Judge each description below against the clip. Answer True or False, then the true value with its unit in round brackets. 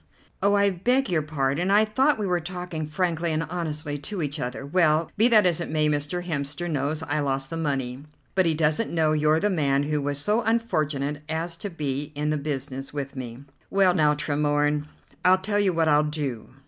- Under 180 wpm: False (205 wpm)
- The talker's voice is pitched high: False (155 Hz)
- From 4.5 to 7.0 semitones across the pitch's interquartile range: False (3.6 semitones)